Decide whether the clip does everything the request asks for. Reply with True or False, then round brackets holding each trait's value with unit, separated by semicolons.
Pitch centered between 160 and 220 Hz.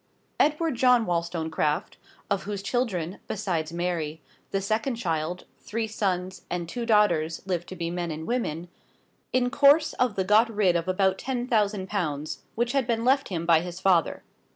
True (190 Hz)